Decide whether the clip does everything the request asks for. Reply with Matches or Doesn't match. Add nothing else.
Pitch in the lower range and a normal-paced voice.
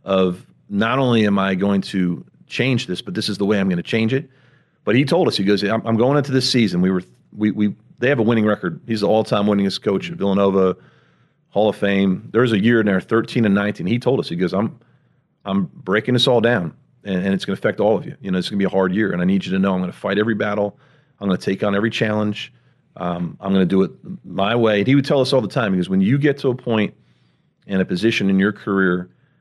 Doesn't match